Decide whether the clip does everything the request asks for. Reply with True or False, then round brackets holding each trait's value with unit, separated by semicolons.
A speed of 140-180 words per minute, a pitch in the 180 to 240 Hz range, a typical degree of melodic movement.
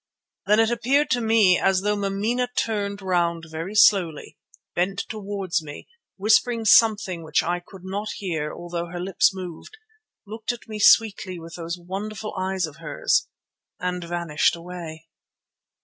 True (150 wpm; 190 Hz; 3.7 semitones)